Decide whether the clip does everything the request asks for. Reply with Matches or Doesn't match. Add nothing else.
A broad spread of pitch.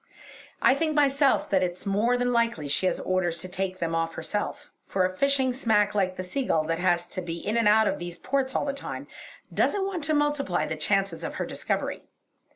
Matches